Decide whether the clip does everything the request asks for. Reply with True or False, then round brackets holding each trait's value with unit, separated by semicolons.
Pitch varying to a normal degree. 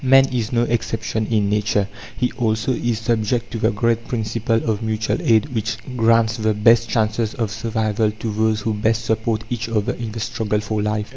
False (1.4 semitones)